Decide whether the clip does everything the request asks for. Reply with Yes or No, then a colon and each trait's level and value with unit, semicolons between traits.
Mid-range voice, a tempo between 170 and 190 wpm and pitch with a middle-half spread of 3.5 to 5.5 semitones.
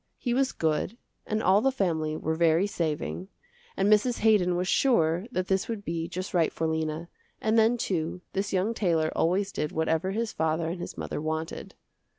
Yes: medium, 180 Hz; average, 185 wpm; average, 4.5 semitones